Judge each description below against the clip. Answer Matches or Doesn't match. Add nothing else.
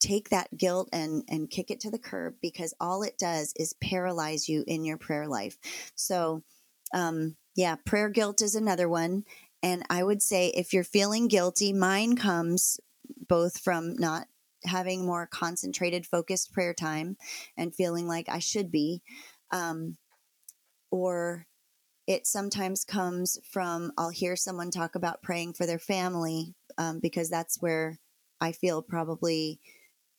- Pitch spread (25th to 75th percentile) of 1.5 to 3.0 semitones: Matches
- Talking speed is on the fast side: Doesn't match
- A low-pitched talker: Doesn't match